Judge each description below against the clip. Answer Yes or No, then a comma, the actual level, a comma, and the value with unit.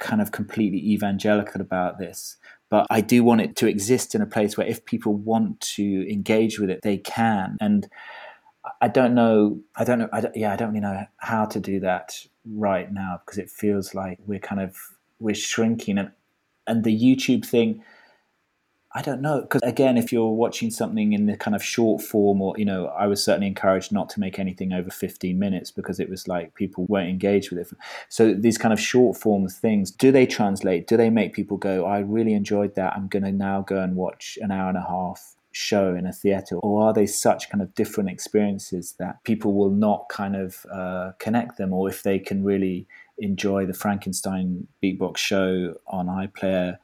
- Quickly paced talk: Yes, fast, 210 wpm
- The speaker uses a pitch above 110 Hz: No, low, 100 Hz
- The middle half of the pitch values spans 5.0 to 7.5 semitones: No, average, 2.9 semitones